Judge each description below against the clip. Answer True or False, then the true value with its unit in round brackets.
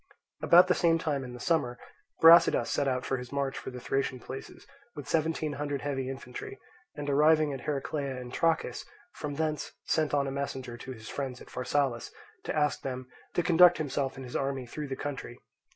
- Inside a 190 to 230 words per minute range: True (195 wpm)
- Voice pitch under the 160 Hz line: True (140 Hz)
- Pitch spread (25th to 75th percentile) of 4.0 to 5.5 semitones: False (3.0 semitones)